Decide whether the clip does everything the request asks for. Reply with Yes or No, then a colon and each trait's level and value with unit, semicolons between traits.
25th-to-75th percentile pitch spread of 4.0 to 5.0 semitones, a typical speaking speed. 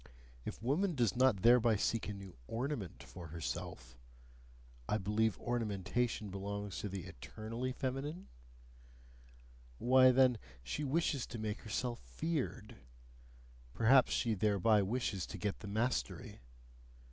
No: average, 4.4 semitones; slow, 125 wpm